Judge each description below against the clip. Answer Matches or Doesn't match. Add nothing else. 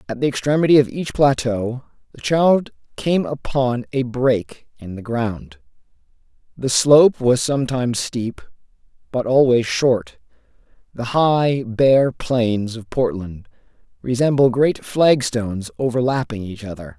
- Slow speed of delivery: Matches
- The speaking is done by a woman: Doesn't match